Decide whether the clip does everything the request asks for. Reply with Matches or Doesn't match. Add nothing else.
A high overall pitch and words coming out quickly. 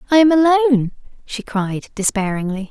Doesn't match